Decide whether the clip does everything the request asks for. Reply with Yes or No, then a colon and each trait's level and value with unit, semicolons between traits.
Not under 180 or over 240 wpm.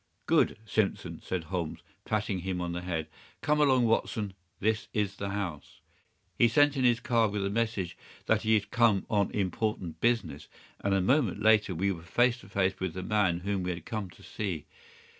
Yes: average, 195 wpm